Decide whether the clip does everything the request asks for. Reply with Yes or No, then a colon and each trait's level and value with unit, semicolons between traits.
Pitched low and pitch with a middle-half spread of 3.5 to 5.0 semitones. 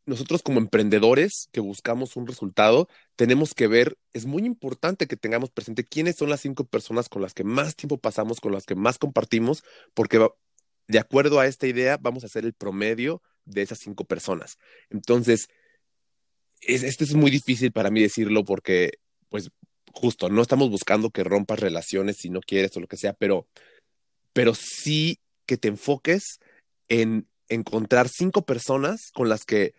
Yes: low, 120 Hz; average, 4.6 semitones